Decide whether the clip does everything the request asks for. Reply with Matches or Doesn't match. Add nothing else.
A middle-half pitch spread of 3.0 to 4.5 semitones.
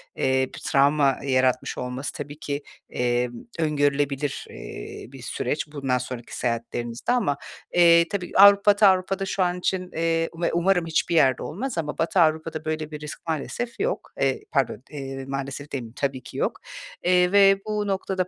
Doesn't match